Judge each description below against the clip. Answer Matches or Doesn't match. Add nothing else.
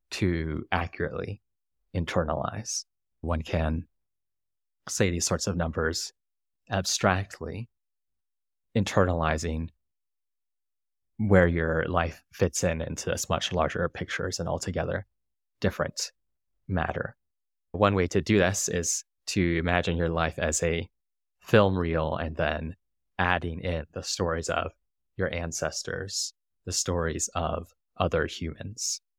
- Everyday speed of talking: Doesn't match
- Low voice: Matches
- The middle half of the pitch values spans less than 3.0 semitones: Matches